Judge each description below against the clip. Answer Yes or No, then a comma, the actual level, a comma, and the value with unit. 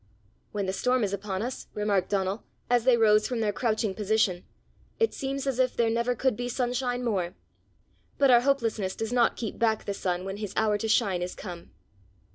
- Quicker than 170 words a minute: Yes, average, 200 wpm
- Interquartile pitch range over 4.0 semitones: No, average, 3.6 semitones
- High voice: Yes, high, 220 Hz